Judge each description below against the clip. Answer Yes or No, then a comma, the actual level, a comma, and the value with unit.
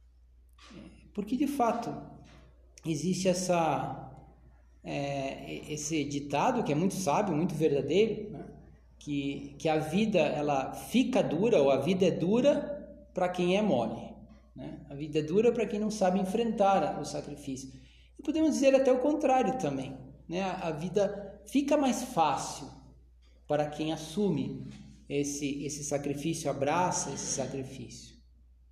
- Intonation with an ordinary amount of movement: No, wide, 6.8 semitones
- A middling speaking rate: Yes, average, 135 wpm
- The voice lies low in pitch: No, medium, 155 Hz